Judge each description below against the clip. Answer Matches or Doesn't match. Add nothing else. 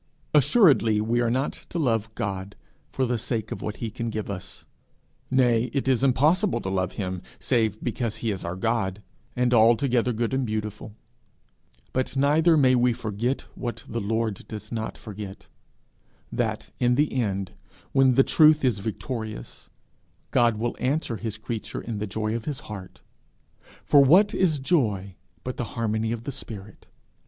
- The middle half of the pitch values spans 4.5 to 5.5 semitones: Doesn't match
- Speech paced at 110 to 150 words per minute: Doesn't match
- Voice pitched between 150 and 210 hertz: Doesn't match